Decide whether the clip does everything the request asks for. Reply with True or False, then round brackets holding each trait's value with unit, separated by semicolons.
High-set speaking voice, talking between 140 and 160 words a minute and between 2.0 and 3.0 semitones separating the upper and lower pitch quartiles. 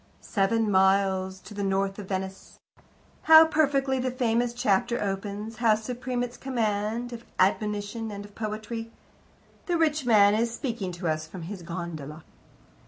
False (215 Hz; 155 wpm; 3.8 semitones)